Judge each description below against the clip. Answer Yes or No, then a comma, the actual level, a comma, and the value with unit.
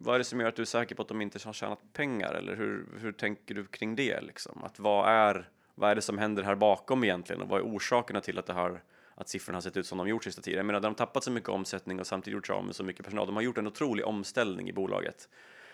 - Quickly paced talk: Yes, fast, 280 wpm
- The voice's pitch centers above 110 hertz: No, low, 105 Hz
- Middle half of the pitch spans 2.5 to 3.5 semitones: Yes, average, 2.8 semitones